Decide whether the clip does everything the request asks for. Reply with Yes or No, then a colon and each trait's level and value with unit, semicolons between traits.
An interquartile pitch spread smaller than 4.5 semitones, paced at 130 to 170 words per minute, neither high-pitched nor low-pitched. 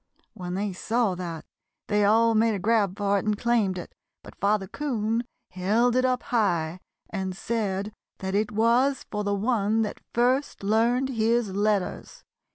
No: average, 3.0 semitones; average, 165 wpm; high, 215 Hz